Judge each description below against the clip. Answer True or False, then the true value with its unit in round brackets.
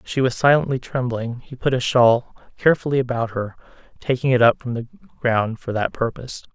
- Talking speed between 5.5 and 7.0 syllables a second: True (5.7 syllables/s)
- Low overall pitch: True (125 Hz)